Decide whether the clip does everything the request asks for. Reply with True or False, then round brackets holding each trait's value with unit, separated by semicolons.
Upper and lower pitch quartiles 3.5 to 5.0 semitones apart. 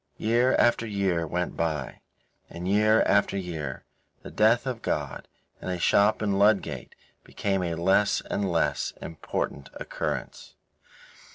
True (4.1 semitones)